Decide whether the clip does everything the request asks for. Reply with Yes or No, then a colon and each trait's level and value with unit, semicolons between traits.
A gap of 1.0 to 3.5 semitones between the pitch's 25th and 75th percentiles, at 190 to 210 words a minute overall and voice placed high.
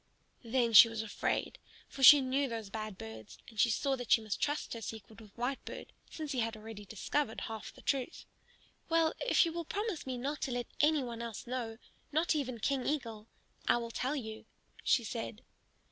No: average, 4.1 semitones; average, 195 wpm; high, 240 Hz